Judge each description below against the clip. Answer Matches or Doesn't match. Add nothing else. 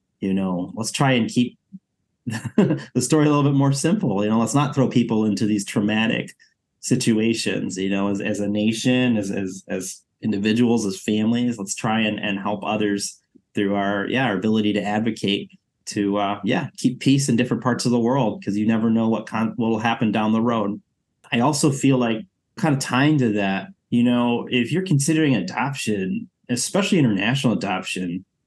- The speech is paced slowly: Doesn't match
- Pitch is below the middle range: Matches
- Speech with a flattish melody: Doesn't match